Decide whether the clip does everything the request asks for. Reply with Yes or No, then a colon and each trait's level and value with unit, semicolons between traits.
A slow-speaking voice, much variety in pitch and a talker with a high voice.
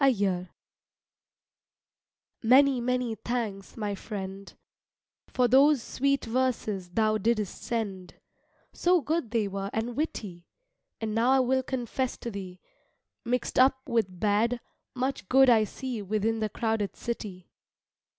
No: slow, 120 wpm; average, 3.9 semitones; high, 230 Hz